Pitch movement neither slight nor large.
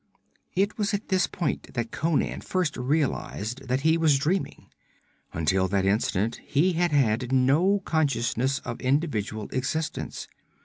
No: wide, 5.8 semitones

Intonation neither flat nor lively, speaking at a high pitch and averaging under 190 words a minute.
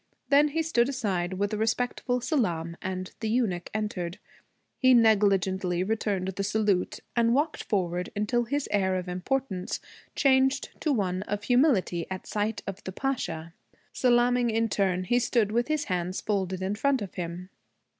Yes: average, 4.9 semitones; high, 210 Hz; average, 160 wpm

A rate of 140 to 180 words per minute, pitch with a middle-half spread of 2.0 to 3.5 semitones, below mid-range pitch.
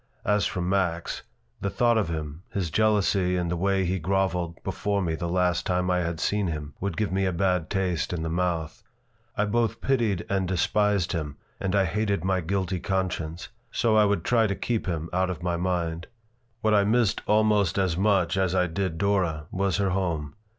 No: average, 200 wpm; average, 2.8 semitones; very low, 95 Hz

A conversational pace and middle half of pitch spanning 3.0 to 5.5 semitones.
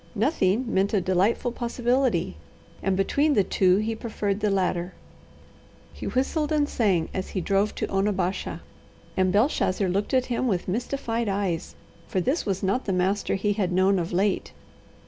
Yes: average, 165 wpm; average, 3.9 semitones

